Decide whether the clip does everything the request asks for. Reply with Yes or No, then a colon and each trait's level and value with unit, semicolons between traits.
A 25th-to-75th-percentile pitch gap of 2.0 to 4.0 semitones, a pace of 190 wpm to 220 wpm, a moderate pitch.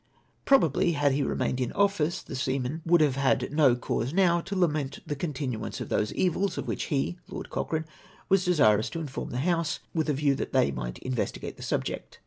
No: average, 4.6 semitones; average, 200 wpm; medium, 150 Hz